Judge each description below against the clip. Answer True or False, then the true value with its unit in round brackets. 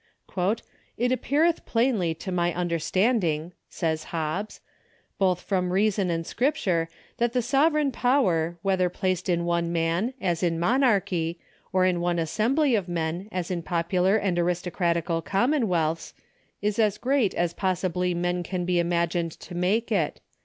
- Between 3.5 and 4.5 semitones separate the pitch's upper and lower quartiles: True (3.9 semitones)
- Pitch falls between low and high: True (180 Hz)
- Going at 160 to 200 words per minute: False (150 wpm)